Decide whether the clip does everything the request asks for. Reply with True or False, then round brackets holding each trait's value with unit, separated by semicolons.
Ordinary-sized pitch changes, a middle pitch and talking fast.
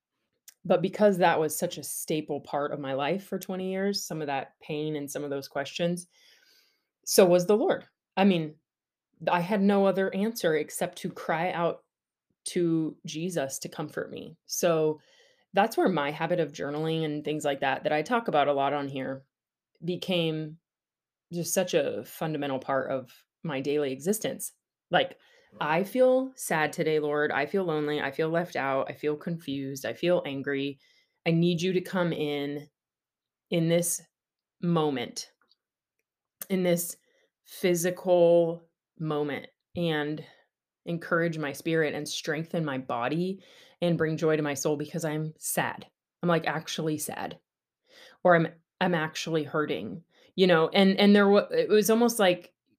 False (3.5 semitones; 165 Hz; 160 wpm)